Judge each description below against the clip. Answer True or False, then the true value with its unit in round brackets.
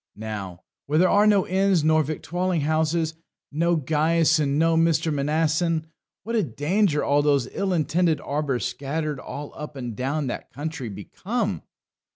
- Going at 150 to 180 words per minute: True (155 wpm)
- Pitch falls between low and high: True (155 Hz)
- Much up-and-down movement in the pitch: False (2.9 semitones)